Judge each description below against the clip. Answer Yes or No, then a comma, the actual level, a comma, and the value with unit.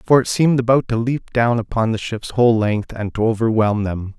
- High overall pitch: No, low, 115 Hz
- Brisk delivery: Yes, fast, 230 wpm